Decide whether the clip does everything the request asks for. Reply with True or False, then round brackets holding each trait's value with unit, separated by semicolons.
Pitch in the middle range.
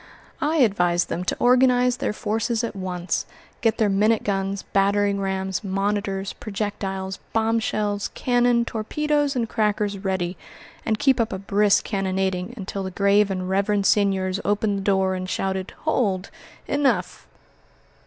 False (200 Hz)